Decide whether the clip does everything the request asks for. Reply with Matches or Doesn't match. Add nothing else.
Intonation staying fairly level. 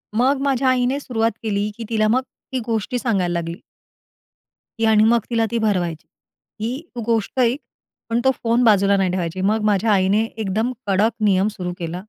Doesn't match